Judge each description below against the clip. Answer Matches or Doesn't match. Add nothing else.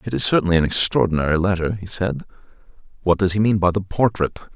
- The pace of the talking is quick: Doesn't match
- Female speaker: Doesn't match